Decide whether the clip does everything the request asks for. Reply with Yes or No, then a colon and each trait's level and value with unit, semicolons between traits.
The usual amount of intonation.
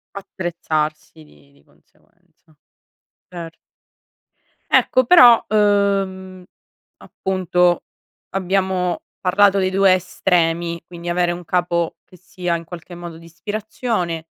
No: narrow, 2.3 semitones